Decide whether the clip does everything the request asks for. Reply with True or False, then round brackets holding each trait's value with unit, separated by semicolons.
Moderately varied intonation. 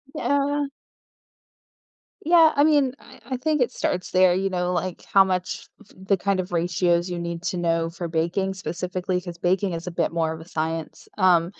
False (2.3 semitones)